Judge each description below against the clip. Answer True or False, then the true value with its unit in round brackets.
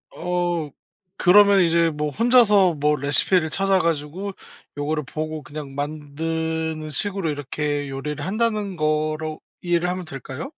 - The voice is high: False (160 Hz)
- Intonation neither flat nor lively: True (3.3 semitones)